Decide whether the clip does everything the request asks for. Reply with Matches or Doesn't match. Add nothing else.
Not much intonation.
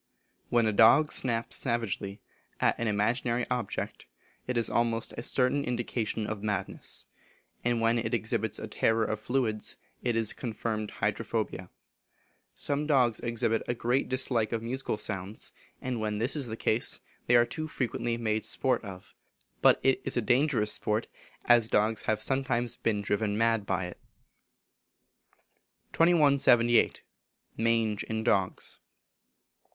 Matches